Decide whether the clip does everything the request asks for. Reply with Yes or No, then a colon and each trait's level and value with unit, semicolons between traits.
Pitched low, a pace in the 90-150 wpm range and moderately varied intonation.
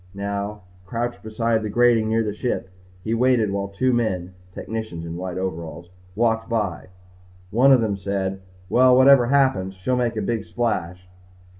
No: low, 110 Hz; average, 160 wpm; average, 3.9 semitones